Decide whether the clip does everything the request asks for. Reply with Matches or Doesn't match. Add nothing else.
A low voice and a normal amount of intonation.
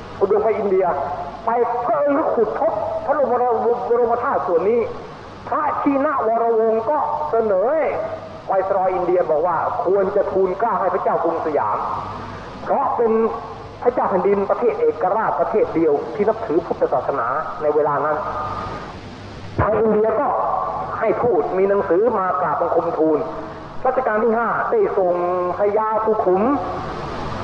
Doesn't match